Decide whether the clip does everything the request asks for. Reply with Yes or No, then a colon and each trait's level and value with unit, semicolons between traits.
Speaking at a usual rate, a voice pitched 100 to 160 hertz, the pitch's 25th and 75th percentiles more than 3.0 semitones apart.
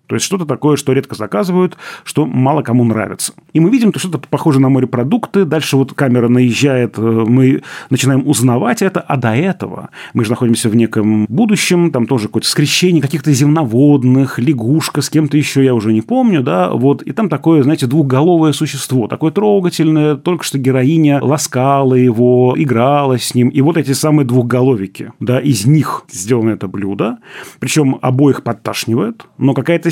No: fast, 170 wpm; low, 135 Hz; average, 4.1 semitones